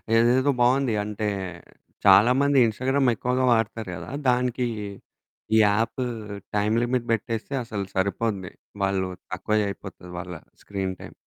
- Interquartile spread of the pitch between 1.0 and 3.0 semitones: No, average, 4.0 semitones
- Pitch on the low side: Yes, low, 115 Hz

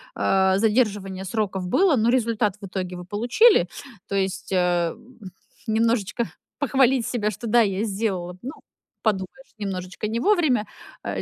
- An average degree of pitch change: Yes, average, 3.9 semitones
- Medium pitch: No, high, 215 Hz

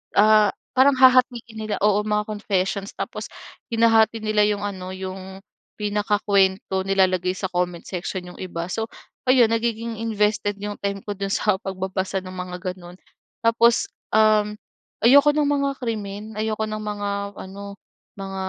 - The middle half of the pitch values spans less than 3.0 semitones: Yes, narrow, 2.5 semitones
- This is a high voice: Yes, high, 205 Hz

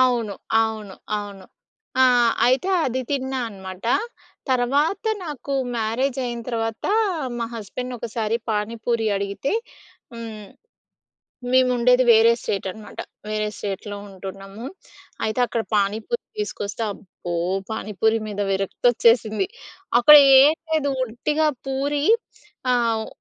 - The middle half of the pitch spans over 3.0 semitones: Yes, average, 3.5 semitones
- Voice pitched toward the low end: No, high, 230 Hz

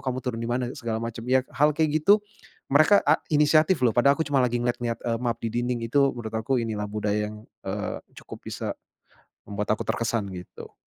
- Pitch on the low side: Yes, low, 120 Hz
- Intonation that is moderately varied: Yes, average, 4.0 semitones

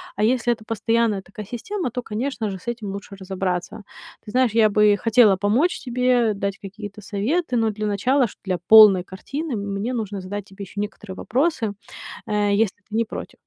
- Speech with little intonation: No, average, 3.1 semitones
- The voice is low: No, high, 215 Hz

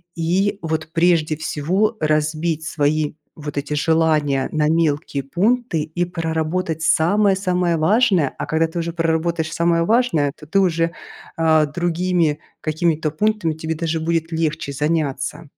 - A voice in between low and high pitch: Yes, medium, 160 Hz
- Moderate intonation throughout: No, narrow, 2.0 semitones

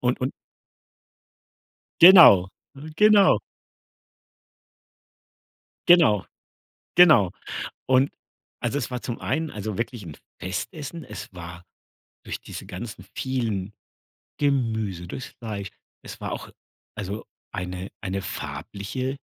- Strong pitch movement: Yes, wide, 6.4 semitones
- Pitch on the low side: Yes, low, 115 Hz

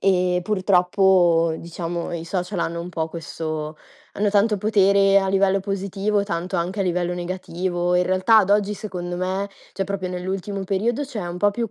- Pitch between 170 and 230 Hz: Yes, medium, 185 Hz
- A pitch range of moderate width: No, narrow, 2.2 semitones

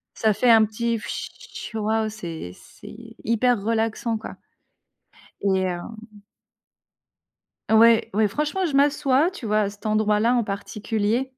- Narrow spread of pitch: Yes, narrow, 1.9 semitones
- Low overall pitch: No, high, 220 Hz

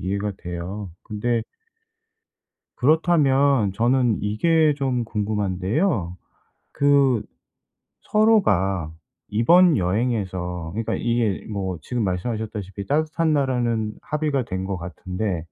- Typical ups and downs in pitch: No, wide, 6.6 semitones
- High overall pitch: No, low, 110 Hz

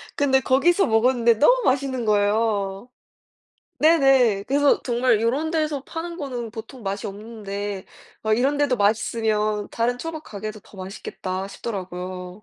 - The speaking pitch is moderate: No, high, 230 Hz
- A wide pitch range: No, average, 4.8 semitones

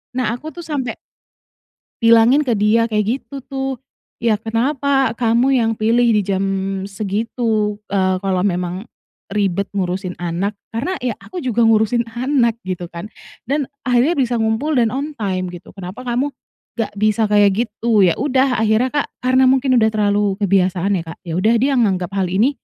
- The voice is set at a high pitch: Yes, high, 225 Hz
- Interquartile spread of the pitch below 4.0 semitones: No, average, 4.3 semitones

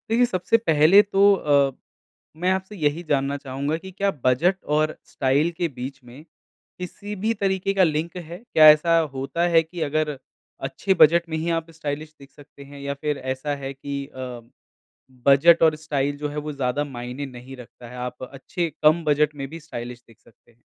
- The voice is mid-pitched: Yes, medium, 150 Hz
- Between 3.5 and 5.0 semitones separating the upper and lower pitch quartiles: Yes, average, 3.8 semitones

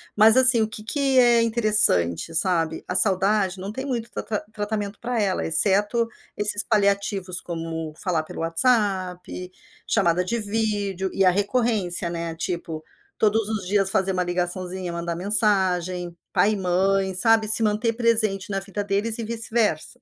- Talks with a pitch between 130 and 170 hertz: No, high, 200 Hz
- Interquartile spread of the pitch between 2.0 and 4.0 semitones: Yes, average, 3.4 semitones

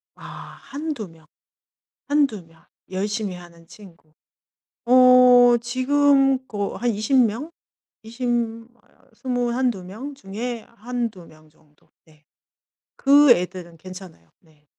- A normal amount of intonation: No, wide, 6.1 semitones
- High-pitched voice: Yes, high, 220 Hz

